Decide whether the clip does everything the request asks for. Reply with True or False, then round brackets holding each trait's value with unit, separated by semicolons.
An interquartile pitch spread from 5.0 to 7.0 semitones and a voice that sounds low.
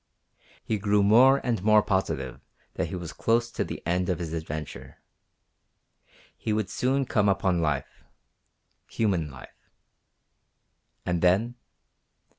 False (4.6 semitones; 95 Hz)